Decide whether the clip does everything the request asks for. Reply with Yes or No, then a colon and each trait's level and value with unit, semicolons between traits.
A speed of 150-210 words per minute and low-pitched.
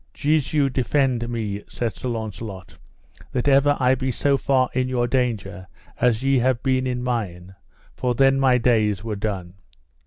Yes: average, 160 wpm; low, 125 Hz